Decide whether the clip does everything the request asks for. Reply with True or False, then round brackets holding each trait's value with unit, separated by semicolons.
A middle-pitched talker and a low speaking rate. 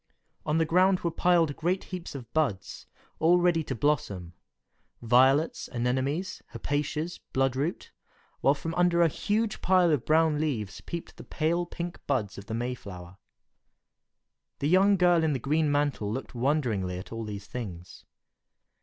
False (145 Hz; 155 wpm)